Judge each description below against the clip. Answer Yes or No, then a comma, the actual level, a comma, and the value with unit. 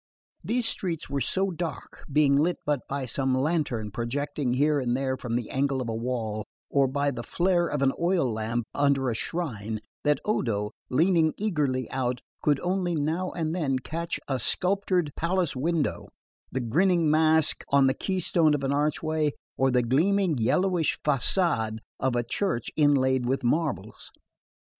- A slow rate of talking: No, average, 160 wpm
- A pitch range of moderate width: Yes, average, 4.7 semitones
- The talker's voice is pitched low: No, medium, 145 Hz